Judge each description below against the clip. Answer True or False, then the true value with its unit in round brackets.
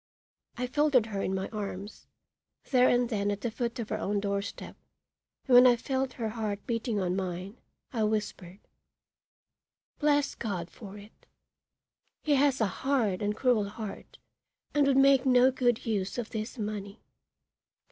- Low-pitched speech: False (220 Hz)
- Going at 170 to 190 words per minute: False (155 wpm)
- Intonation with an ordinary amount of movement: True (3.8 semitones)